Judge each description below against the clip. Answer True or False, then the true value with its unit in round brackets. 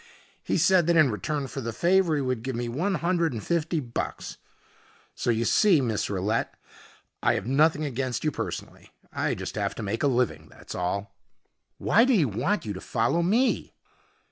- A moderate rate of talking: True (190 wpm)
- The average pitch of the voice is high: False (135 Hz)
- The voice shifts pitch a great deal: True (6.8 semitones)